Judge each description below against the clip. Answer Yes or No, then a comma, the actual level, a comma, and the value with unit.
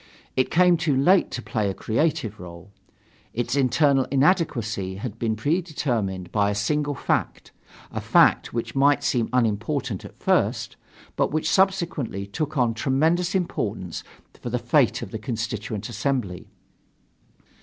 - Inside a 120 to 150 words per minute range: Yes, average, 140 wpm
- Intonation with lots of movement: Yes, wide, 5.9 semitones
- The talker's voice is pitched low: Yes, low, 125 Hz